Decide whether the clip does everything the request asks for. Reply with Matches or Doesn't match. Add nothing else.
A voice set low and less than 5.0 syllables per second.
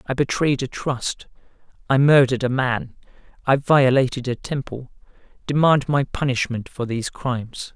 Matches